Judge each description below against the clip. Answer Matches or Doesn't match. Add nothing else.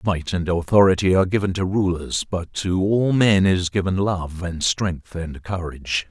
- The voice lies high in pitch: Doesn't match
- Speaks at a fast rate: Doesn't match